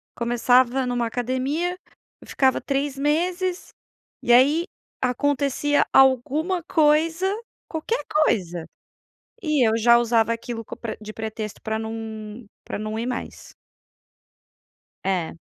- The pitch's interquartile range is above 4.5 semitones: Yes, average, 4.9 semitones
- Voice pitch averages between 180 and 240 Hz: No, very high, 250 Hz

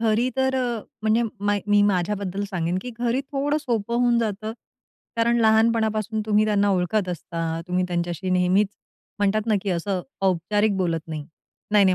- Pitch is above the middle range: Yes, high, 205 Hz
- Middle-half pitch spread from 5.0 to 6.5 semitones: No, average, 3.7 semitones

